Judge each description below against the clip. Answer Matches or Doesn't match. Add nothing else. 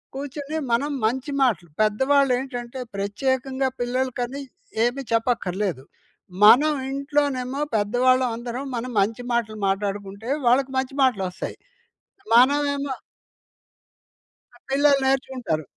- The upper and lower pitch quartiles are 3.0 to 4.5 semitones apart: Matches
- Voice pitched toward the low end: Doesn't match